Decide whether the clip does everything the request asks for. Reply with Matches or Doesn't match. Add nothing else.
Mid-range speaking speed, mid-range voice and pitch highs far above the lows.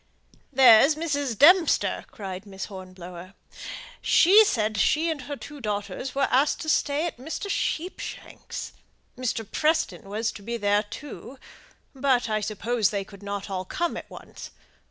Doesn't match